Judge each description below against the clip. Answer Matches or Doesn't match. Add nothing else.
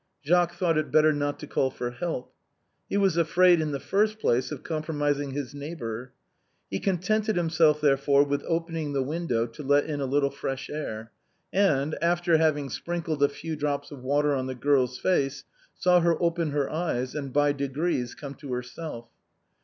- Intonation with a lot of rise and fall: Doesn't match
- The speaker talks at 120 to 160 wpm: Doesn't match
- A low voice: Doesn't match